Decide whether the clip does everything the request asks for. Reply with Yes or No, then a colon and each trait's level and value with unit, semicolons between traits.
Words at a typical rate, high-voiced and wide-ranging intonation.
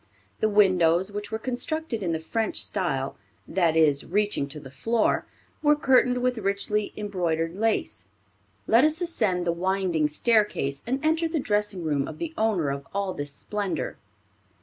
Yes: average, 160 wpm; high, 200 Hz; wide, 5.7 semitones